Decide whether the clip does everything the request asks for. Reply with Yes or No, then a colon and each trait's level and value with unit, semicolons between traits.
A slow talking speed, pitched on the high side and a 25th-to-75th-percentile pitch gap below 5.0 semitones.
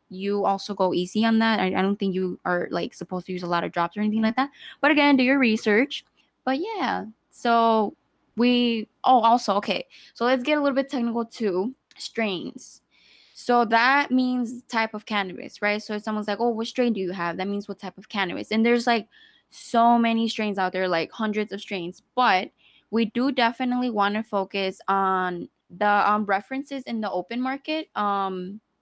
No: average, 200 wpm; high, 220 Hz; average, 3.7 semitones